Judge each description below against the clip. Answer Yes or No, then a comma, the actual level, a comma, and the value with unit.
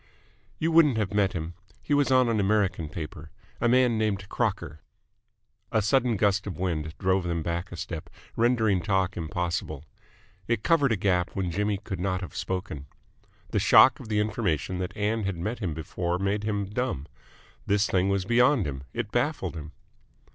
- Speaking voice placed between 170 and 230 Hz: No, low, 100 Hz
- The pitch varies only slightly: No, average, 4.1 semitones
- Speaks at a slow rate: No, average, 175 wpm